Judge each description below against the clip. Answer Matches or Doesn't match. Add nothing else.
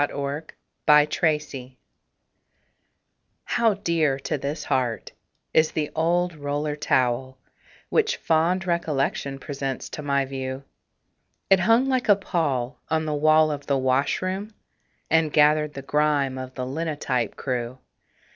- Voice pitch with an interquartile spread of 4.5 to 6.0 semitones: Doesn't match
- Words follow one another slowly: Matches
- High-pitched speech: Doesn't match